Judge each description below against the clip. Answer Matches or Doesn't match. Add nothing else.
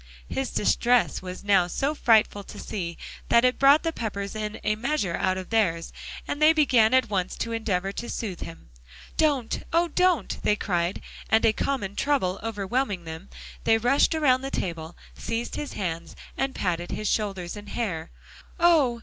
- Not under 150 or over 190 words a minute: Matches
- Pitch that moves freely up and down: Matches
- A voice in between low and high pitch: Doesn't match